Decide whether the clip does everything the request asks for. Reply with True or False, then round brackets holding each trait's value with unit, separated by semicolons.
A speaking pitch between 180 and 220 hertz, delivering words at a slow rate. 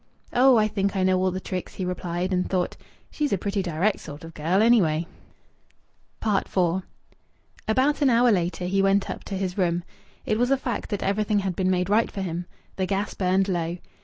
False (190 Hz; 200 wpm)